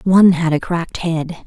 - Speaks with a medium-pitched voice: Yes, medium, 170 Hz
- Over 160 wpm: Yes, fast, 205 wpm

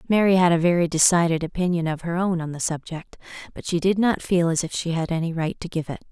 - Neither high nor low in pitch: Yes, medium, 170 Hz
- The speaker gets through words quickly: Yes, fast, 255 wpm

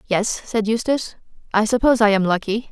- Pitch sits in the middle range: No, high, 220 Hz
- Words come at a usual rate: Yes, average, 175 wpm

